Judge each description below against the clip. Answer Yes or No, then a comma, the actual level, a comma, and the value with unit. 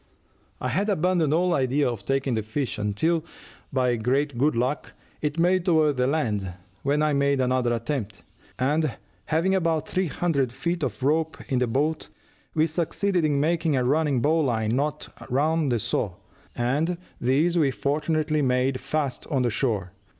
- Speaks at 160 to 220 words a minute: Yes, average, 165 wpm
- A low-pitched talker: No, medium, 145 Hz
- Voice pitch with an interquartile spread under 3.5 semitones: No, average, 4.0 semitones